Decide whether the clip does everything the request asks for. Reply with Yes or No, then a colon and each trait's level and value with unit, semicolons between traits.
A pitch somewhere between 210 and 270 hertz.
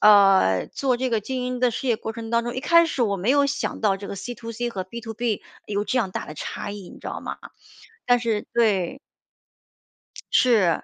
Yes: high, 230 Hz